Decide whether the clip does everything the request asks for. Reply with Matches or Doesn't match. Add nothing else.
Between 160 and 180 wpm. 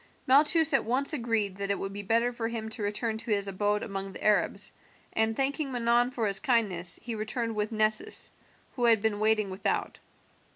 Doesn't match